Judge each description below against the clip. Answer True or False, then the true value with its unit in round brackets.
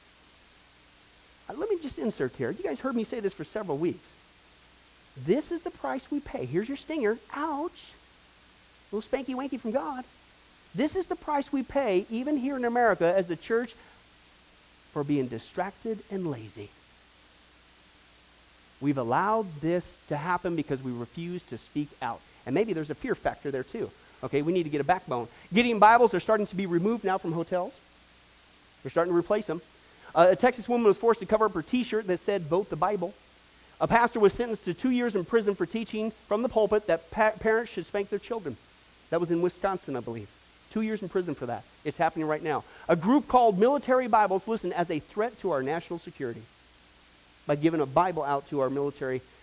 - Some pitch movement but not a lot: False (9.0 semitones)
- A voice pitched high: False (180 Hz)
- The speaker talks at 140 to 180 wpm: False (200 wpm)